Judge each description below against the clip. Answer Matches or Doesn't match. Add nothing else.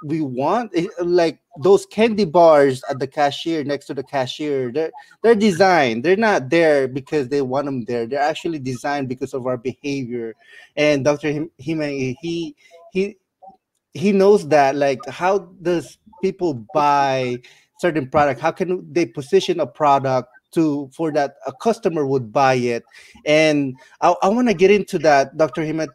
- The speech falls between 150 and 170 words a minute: Matches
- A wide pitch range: Doesn't match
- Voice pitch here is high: Doesn't match